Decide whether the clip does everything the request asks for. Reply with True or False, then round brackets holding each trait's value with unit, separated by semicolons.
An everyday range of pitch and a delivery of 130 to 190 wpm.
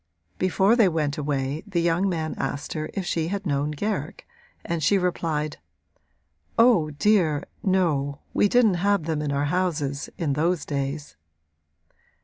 True (4.2 semitones; 145 wpm)